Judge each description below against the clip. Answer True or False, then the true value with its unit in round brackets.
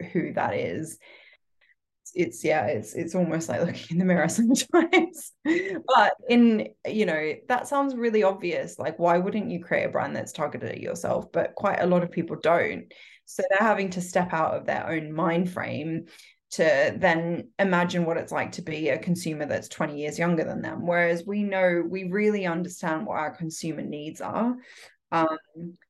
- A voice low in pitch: False (175 Hz)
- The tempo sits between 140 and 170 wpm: False (185 wpm)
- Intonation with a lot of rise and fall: False (4.5 semitones)